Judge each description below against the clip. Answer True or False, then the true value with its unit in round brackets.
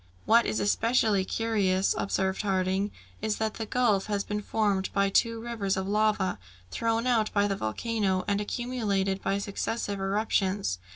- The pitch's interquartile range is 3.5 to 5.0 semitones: False (2.6 semitones)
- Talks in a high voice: True (205 Hz)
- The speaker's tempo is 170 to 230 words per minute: False (155 wpm)